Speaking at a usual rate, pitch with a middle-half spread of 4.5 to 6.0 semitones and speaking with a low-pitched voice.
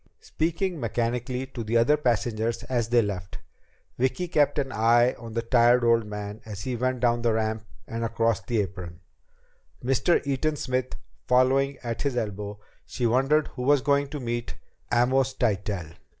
No: average, 165 wpm; average, 2.9 semitones; low, 120 Hz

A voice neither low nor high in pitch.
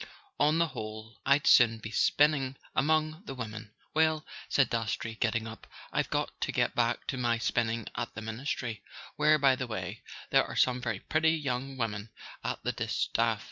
No: low, 125 Hz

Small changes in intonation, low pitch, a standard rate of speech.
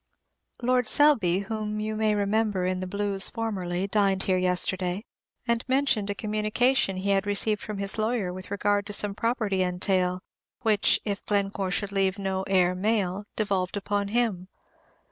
No: narrow, 2.3 semitones; high, 200 Hz; average, 160 wpm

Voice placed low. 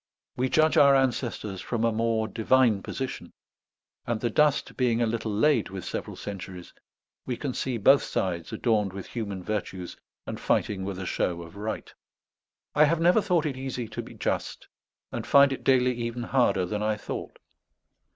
Yes: low, 115 Hz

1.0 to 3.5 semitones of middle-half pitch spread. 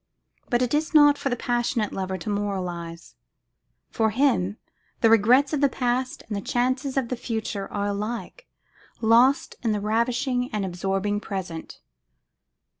No: average, 4.0 semitones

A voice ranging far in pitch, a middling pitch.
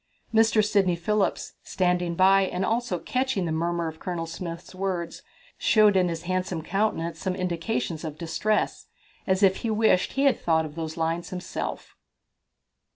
No: average, 3.3 semitones; medium, 180 Hz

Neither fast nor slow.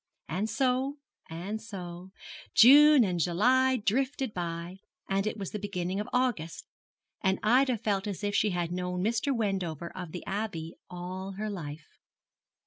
Yes: average, 150 wpm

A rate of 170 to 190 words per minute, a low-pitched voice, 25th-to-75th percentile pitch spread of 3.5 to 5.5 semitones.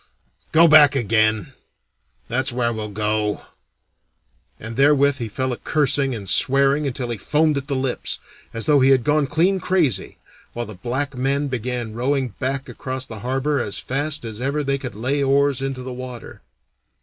No: average, 175 wpm; low, 130 Hz; average, 3.1 semitones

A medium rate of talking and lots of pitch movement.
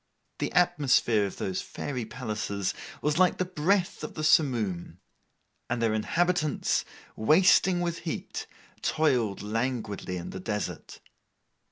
No: slow, 125 wpm; wide, 7.9 semitones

